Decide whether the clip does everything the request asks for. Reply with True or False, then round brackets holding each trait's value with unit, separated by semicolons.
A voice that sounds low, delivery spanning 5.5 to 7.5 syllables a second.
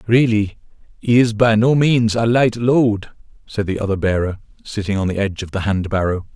False (110 Hz; 5.2 syllables/s)